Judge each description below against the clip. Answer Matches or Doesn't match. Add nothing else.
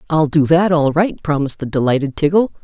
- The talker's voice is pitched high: Doesn't match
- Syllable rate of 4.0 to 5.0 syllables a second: Doesn't match